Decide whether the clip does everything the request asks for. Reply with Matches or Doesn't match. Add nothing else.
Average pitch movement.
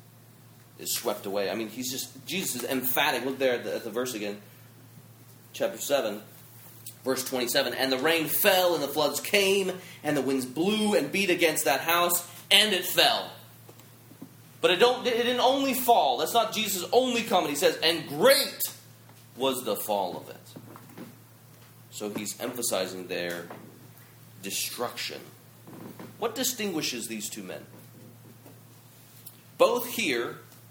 Doesn't match